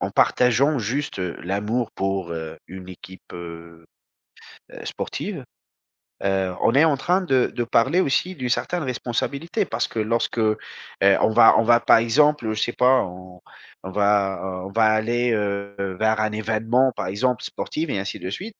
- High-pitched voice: No, low, 110 Hz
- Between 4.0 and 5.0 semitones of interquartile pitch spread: Yes, average, 4.7 semitones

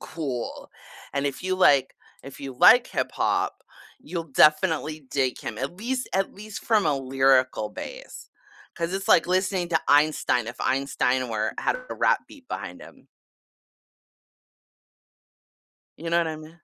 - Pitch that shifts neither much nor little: No, wide, 5.7 semitones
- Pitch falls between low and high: Yes, medium, 155 Hz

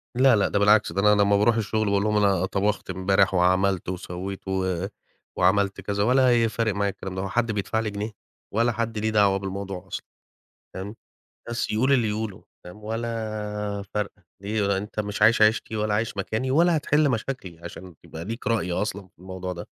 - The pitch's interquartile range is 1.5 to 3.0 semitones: Yes, narrow, 2.6 semitones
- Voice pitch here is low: Yes, low, 105 Hz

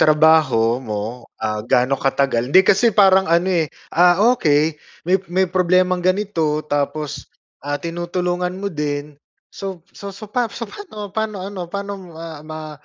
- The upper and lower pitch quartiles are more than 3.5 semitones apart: Yes, average, 4.5 semitones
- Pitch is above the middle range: No, medium, 170 Hz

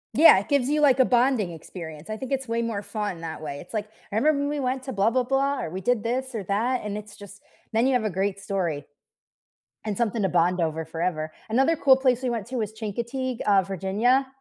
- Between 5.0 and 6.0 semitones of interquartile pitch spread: Yes, average, 5.3 semitones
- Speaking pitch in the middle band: No, high, 220 Hz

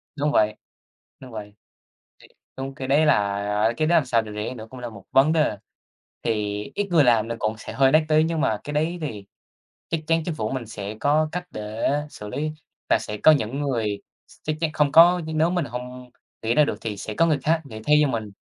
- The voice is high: No, low, 135 Hz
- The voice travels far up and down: Yes, wide, 6.0 semitones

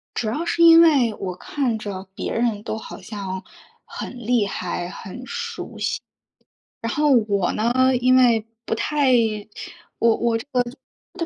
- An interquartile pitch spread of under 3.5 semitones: No, average, 4.2 semitones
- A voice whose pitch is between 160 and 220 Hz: No, high, 230 Hz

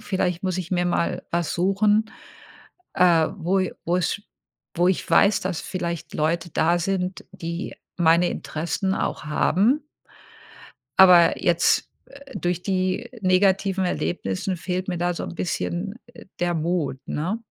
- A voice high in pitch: No, medium, 180 Hz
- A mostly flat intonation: Yes, narrow, 1.9 semitones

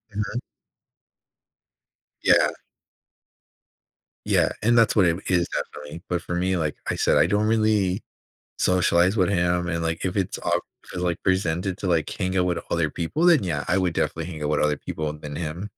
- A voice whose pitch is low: Yes, very low, 90 Hz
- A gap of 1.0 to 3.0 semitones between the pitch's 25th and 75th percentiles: Yes, average, 2.7 semitones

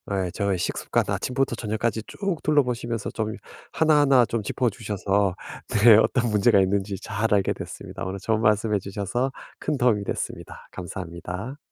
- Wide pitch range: No, average, 3.7 semitones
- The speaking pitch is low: Yes, low, 110 Hz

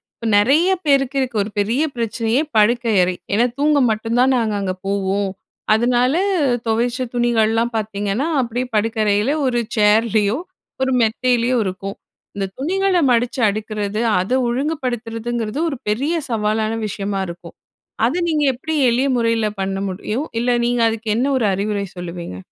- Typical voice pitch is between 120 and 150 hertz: No, high, 230 Hz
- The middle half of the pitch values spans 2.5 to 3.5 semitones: Yes, average, 3.2 semitones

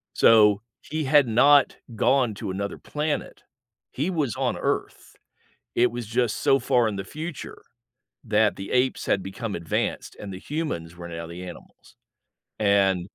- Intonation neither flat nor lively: No, wide, 5.8 semitones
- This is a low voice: Yes, low, 110 Hz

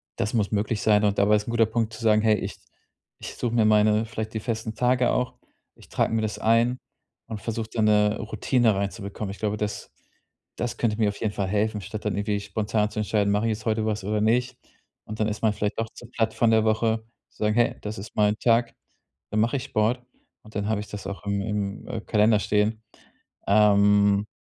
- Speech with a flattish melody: Yes, narrow, 1.4 semitones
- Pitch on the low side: Yes, low, 110 Hz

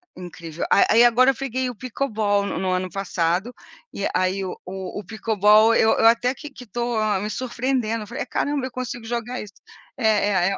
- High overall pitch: Yes, high, 220 Hz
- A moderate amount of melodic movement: Yes, average, 4.0 semitones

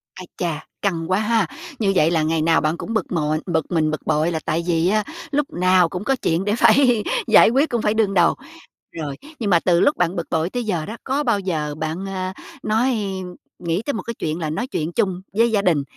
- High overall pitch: No, medium, 180 Hz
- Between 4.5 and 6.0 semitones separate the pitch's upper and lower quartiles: Yes, average, 4.9 semitones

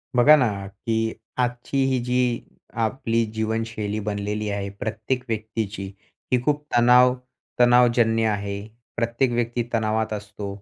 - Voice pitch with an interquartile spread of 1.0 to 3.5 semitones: Yes, narrow, 2.5 semitones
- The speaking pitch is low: Yes, low, 115 Hz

